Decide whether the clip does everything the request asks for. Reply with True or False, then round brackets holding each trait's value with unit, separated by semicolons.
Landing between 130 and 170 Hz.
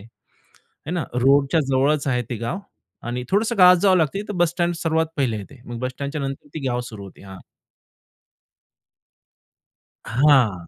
True (140 Hz)